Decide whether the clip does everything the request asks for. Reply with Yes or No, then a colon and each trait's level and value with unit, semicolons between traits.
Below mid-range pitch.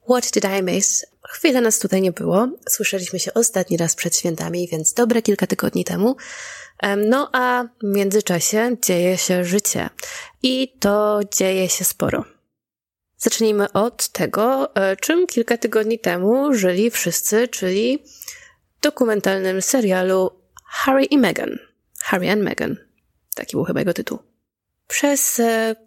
No: high, 215 Hz